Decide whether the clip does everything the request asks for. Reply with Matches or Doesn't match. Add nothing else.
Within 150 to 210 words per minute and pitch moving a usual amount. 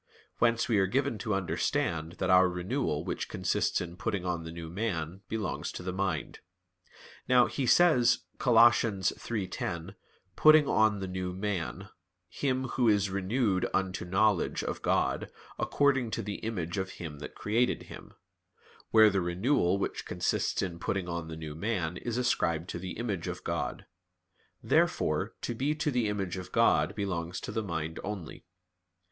Matches